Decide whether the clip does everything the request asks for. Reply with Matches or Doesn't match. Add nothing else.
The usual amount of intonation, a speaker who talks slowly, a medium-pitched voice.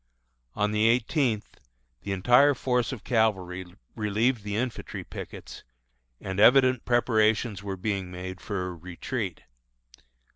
Doesn't match